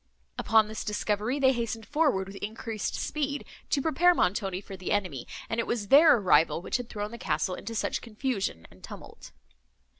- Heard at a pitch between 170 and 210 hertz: No, high, 220 Hz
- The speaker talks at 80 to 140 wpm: No, average, 180 wpm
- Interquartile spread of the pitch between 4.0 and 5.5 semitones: Yes, average, 4.7 semitones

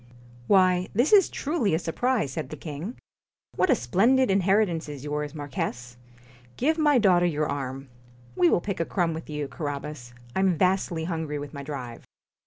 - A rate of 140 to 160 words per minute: No, average, 175 wpm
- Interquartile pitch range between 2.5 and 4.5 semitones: No, average, 5.3 semitones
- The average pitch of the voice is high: No, medium, 165 Hz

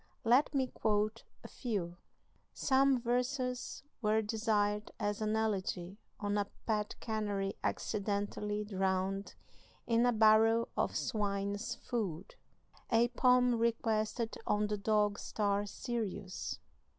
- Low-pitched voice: No, high, 215 Hz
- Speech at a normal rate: No, slow, 115 wpm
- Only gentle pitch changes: Yes, narrow, 2.3 semitones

